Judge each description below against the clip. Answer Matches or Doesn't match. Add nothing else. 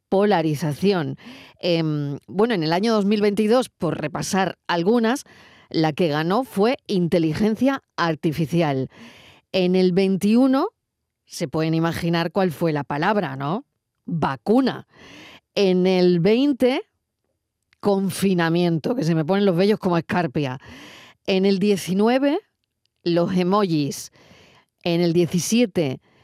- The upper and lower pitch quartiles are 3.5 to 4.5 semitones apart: Matches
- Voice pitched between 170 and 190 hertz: Matches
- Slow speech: Matches